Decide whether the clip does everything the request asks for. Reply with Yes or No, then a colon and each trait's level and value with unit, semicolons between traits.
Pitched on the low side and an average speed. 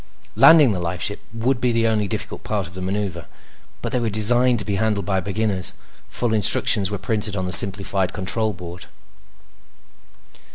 Yes: low, 105 Hz; average, 170 wpm